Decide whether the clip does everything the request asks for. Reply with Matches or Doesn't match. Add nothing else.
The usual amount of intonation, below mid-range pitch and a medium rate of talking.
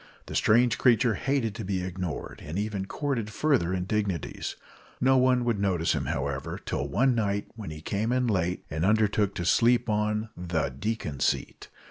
Matches